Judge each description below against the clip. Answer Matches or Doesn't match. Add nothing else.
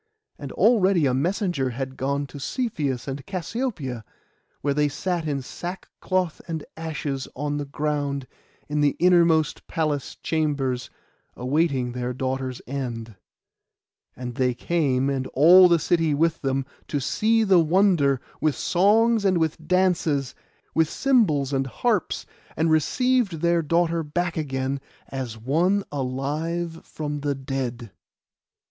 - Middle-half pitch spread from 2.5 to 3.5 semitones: Doesn't match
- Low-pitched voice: Doesn't match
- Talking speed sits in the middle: Doesn't match